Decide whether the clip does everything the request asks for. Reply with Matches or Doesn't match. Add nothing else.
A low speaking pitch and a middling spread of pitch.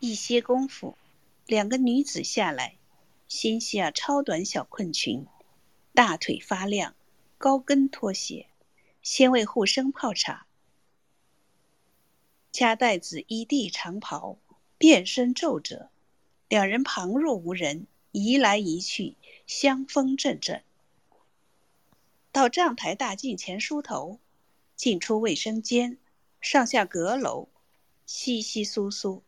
Doesn't match